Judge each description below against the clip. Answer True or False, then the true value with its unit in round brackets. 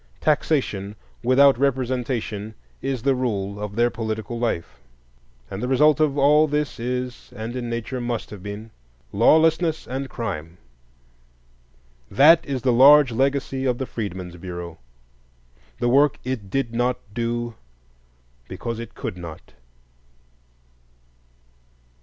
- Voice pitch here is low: True (120 Hz)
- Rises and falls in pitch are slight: False (3.7 semitones)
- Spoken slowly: True (125 wpm)